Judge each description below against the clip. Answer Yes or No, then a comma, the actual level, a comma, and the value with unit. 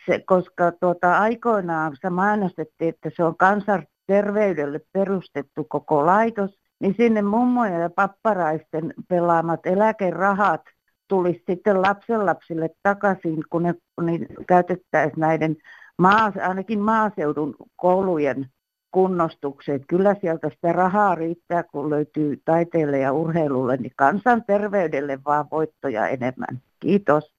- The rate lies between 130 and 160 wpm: No, average, 110 wpm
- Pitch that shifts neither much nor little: Yes, average, 4.2 semitones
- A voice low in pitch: No, medium, 175 Hz